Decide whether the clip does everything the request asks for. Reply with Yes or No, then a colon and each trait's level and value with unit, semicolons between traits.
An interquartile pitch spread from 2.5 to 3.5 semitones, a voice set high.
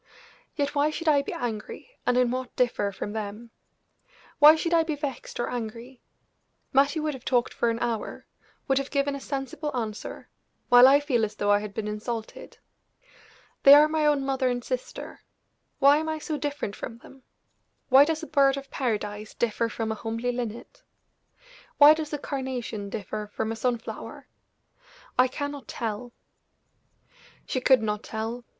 No: average, 4.2 semitones; very high, 250 Hz